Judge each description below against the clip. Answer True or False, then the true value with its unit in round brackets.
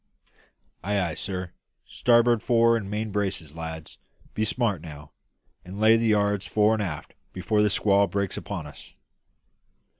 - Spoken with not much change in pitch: False (3.7 semitones)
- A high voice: False (100 Hz)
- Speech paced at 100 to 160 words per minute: True (150 wpm)